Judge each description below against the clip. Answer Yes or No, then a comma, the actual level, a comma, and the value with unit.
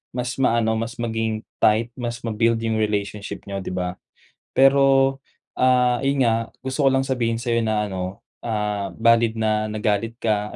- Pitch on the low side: Yes, low, 115 Hz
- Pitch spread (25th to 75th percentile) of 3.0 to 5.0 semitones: No, narrow, 2.5 semitones